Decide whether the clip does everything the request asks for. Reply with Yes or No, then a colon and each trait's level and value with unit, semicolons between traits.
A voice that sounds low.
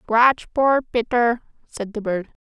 No: high, 230 Hz